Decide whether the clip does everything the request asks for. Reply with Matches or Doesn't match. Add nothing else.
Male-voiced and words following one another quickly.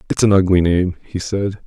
Matches